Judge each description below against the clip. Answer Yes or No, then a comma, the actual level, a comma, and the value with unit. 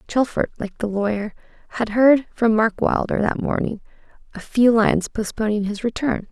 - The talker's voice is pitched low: No, high, 220 Hz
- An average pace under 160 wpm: Yes, average, 150 wpm